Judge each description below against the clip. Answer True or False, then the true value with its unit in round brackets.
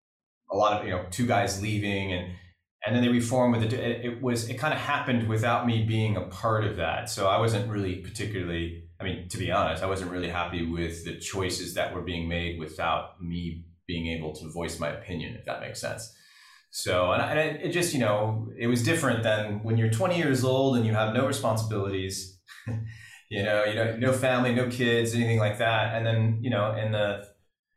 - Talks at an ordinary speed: False (215 wpm)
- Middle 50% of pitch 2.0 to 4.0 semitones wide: False (4.6 semitones)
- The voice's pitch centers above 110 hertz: False (105 Hz)